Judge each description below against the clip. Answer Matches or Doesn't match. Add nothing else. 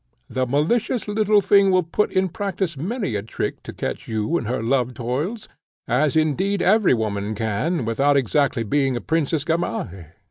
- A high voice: Doesn't match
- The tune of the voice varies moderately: Doesn't match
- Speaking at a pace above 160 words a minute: Matches